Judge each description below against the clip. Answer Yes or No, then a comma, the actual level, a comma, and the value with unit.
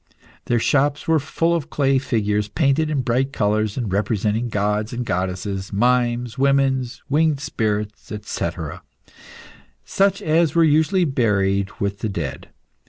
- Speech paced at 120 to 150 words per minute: Yes, slow, 135 wpm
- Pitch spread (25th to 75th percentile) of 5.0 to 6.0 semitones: Yes, average, 5.3 semitones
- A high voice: No, low, 120 Hz